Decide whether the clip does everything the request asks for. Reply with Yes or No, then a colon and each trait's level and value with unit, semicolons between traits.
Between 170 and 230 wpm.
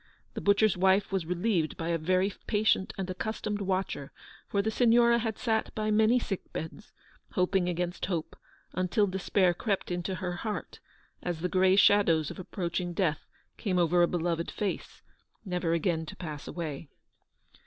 No: average, 160 wpm